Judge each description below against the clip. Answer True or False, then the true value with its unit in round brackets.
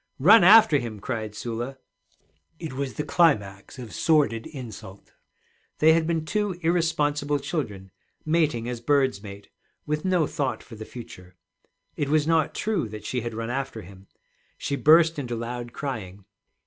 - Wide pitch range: True (5.7 semitones)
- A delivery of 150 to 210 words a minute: True (155 wpm)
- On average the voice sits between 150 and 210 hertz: False (135 Hz)